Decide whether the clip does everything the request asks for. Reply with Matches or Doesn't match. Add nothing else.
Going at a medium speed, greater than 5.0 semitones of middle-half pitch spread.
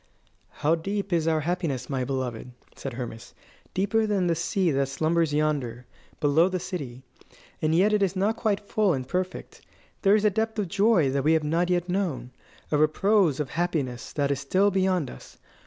Matches